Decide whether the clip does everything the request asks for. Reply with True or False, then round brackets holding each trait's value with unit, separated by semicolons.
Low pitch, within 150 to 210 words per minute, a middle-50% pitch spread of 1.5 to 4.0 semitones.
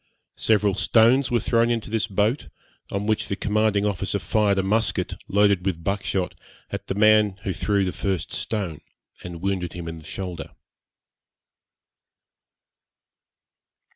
False (100 Hz; 140 wpm; 2.4 semitones)